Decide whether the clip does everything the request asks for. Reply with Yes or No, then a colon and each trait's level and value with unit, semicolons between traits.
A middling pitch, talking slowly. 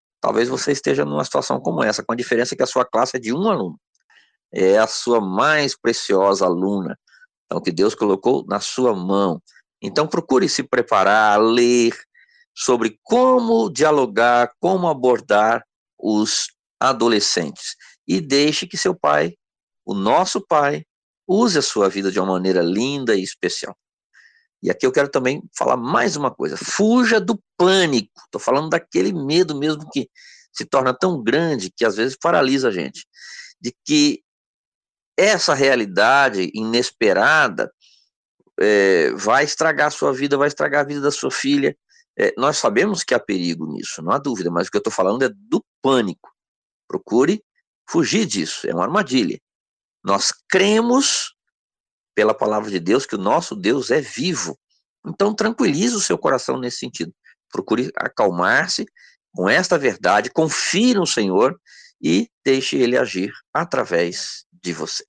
No: medium, 150 Hz; average, 155 wpm